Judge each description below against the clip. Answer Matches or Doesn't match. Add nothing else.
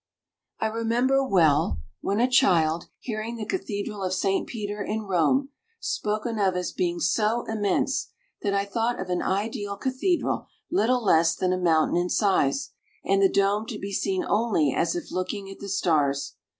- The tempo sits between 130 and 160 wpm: Doesn't match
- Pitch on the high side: Matches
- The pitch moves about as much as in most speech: Matches